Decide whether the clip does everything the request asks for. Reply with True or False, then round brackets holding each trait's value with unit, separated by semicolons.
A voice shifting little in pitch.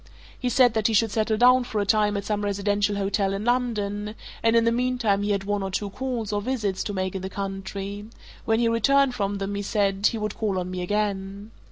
True (2.3 semitones)